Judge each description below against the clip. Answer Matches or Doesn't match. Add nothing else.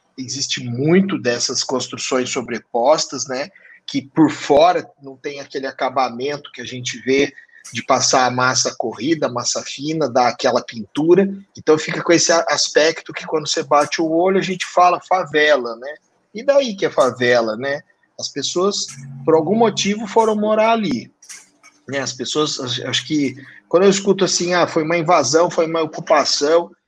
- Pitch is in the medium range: Matches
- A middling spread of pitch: Matches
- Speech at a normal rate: Matches